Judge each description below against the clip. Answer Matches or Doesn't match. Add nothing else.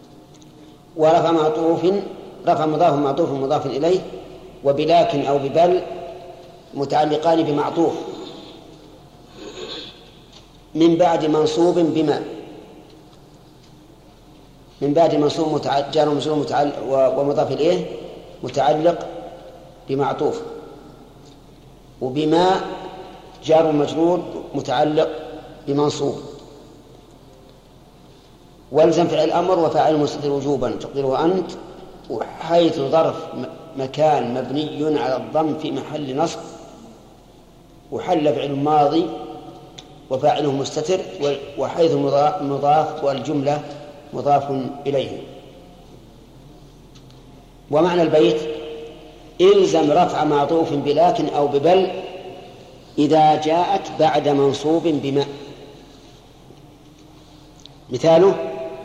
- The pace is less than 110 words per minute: Matches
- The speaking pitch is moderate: Matches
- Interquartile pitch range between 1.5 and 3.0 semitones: Matches